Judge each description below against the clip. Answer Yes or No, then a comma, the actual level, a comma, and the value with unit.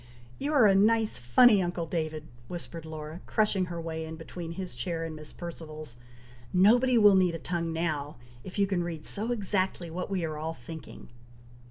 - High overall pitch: No, medium, 170 Hz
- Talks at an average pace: Yes, average, 185 wpm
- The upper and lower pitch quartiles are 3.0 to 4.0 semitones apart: Yes, average, 3.4 semitones